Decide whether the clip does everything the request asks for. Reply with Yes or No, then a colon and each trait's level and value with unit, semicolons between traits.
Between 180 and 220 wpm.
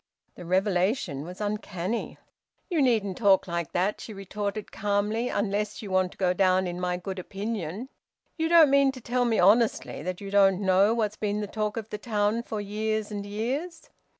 Yes: average, 185 wpm